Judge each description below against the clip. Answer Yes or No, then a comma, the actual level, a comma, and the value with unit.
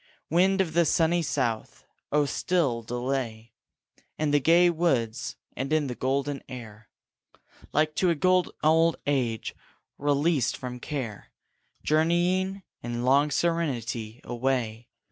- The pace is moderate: No, slow, 125 wpm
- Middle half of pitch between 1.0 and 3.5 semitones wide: No, wide, 5.4 semitones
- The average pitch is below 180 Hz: Yes, medium, 140 Hz